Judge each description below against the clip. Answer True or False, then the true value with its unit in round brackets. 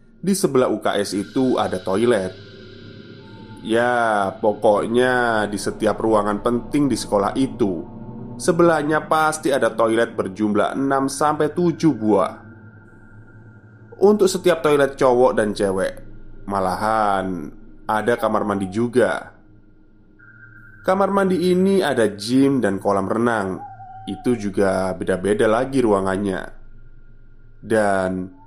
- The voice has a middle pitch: False (110 Hz)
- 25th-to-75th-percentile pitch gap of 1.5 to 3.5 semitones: False (3.9 semitones)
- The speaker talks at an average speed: True (100 wpm)